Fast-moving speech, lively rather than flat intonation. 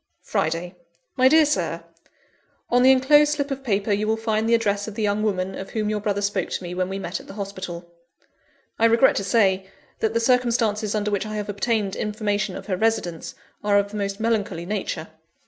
No: fast, 210 wpm; narrow, 2.6 semitones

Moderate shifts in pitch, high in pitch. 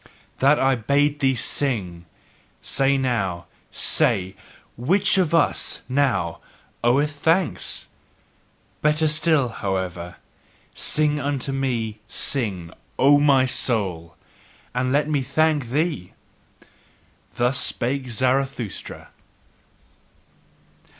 No: average, 4.5 semitones; low, 135 Hz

